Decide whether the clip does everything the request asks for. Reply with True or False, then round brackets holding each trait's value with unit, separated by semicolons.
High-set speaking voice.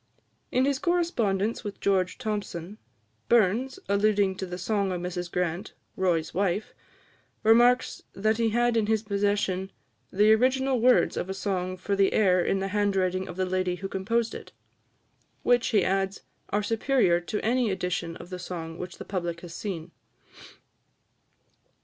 True (195 Hz)